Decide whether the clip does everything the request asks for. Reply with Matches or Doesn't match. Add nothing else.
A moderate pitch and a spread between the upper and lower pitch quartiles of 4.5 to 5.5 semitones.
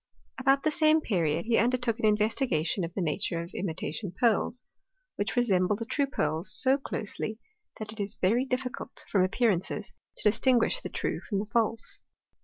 Doesn't match